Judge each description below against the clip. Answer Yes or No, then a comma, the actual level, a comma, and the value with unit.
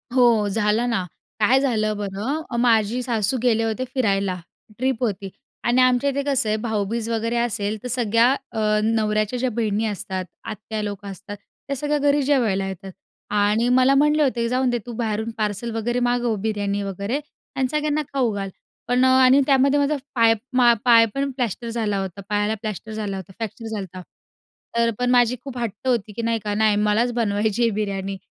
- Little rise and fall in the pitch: No, average, 3.2 semitones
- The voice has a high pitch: Yes, high, 225 Hz